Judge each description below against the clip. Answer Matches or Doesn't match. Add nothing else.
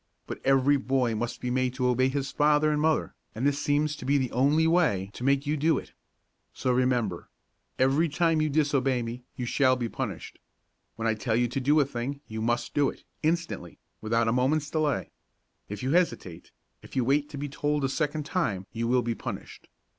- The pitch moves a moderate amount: Matches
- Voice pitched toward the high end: Doesn't match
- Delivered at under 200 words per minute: Doesn't match